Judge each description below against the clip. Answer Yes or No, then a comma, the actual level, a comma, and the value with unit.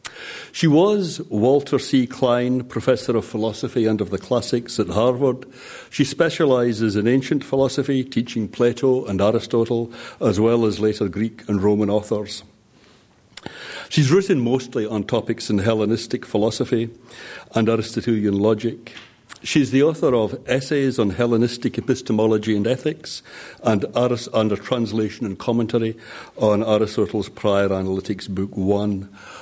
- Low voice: Yes, low, 115 Hz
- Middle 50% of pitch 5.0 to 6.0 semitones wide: No, average, 2.9 semitones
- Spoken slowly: Yes, slow, 130 wpm